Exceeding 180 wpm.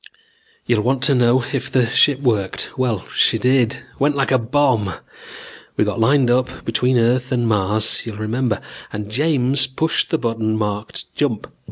No: average, 165 wpm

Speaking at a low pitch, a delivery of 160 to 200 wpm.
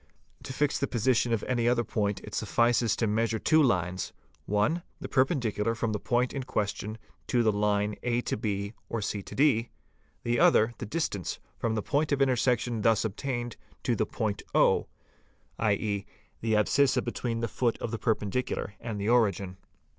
Yes: low, 115 Hz; average, 170 wpm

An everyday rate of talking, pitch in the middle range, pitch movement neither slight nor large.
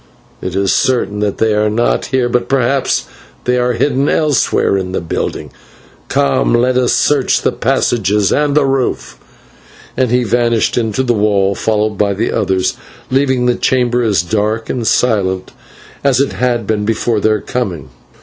No: average, 165 wpm; low, 115 Hz; average, 3.5 semitones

